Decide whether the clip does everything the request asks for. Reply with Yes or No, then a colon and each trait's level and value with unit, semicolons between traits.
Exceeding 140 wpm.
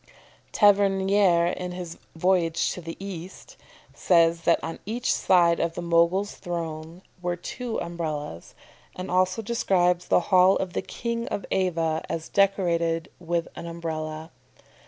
No: slow, 135 wpm